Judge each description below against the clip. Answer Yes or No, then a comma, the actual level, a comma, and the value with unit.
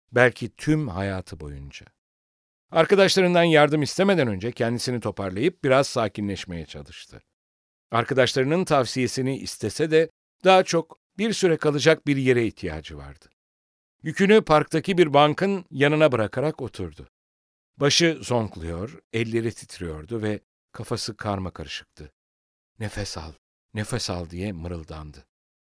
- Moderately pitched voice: No, low, 115 Hz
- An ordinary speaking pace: No, slow, 110 wpm